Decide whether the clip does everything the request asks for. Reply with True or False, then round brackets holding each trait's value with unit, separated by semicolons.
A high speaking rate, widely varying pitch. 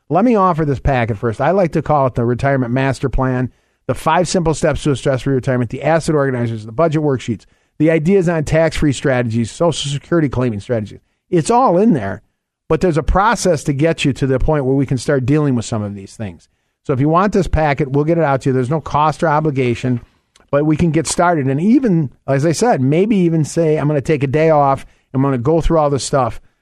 False (245 wpm; 4.0 semitones)